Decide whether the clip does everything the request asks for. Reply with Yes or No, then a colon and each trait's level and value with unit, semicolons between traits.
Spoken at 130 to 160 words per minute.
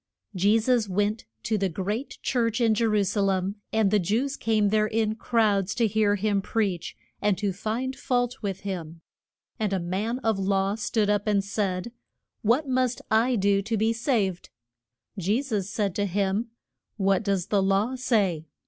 No: average, 175 wpm